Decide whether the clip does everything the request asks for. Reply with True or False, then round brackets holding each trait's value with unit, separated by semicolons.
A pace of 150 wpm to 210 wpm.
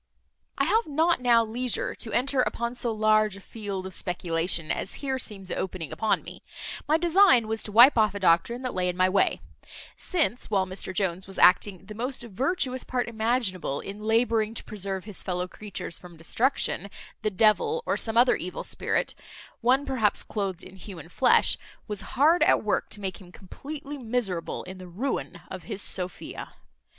True (180 wpm)